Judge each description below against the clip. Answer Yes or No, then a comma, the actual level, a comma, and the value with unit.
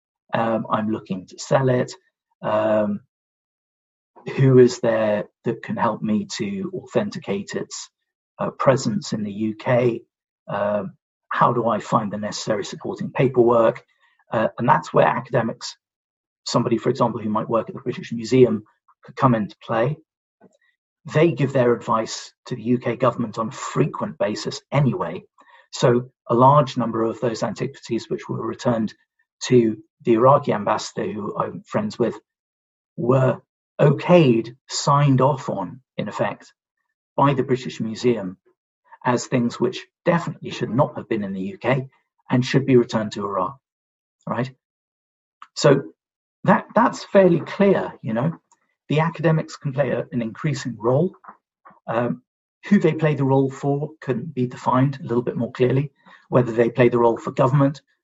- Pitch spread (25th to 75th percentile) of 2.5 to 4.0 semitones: No, wide, 5.5 semitones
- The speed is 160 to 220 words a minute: No, average, 150 wpm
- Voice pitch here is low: Yes, low, 130 Hz